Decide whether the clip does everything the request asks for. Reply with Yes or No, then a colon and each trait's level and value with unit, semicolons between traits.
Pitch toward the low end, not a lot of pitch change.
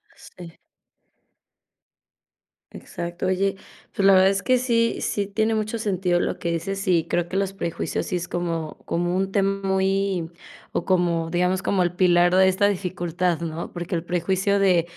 No: medium, 185 Hz; narrow, 2.1 semitones